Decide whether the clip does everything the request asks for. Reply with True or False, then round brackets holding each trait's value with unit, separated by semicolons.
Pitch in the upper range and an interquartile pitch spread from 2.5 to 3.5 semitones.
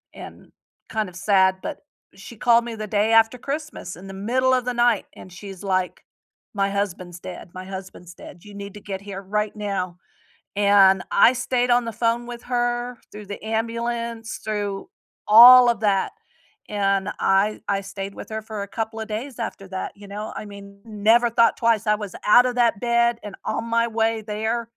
True (215 Hz; 2.9 semitones)